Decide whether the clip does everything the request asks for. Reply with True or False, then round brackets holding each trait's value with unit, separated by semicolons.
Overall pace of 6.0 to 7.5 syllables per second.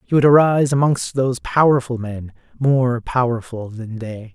False (4.8 syllables/s)